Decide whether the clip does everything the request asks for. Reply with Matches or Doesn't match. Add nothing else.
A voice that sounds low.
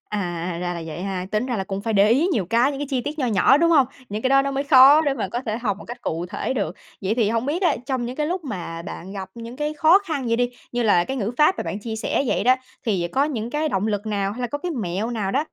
Doesn't match